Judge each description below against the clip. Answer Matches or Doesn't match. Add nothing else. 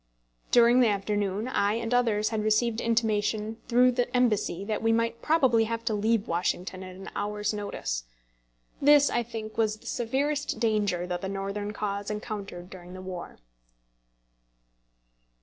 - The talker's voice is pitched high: Matches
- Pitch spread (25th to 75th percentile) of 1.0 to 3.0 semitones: Matches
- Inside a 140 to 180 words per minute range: Matches